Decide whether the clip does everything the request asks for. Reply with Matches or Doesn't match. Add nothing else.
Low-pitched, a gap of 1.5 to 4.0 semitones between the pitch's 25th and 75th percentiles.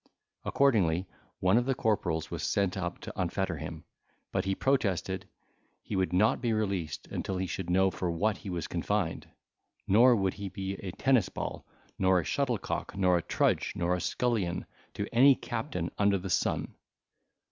Matches